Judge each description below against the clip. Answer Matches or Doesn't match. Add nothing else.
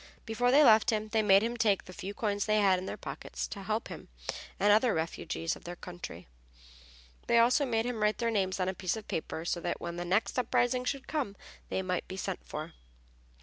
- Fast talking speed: Matches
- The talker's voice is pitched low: Doesn't match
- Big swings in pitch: Doesn't match